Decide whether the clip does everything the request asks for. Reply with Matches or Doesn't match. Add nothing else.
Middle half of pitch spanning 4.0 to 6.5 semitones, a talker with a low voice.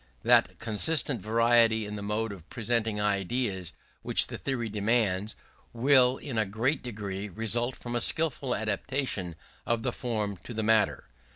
Doesn't match